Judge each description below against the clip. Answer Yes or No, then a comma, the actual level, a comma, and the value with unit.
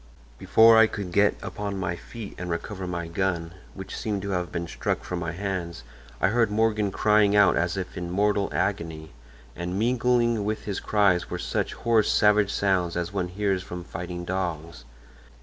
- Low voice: Yes, very low, 95 Hz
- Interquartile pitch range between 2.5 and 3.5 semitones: Yes, average, 2.9 semitones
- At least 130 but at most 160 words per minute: No, average, 180 wpm